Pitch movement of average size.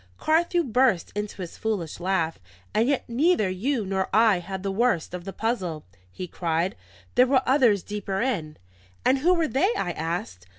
No: wide, 6.1 semitones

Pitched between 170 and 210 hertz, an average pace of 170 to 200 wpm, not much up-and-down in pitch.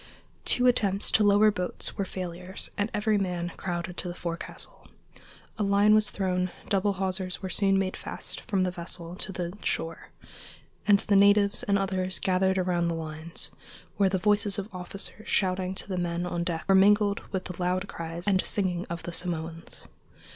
Yes: medium, 185 Hz; average, 180 wpm; narrow, 2.3 semitones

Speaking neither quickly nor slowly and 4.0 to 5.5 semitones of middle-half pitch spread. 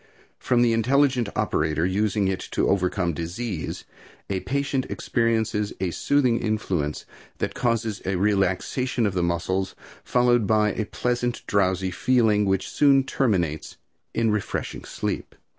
No: slow, 130 wpm; average, 4.5 semitones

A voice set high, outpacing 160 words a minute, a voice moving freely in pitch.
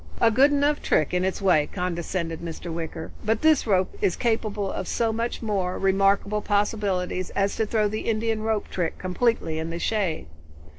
No: high, 200 Hz; average, 180 wpm; average, 3.6 semitones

